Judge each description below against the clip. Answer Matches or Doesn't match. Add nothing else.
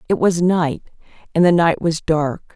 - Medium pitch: Matches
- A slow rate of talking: Doesn't match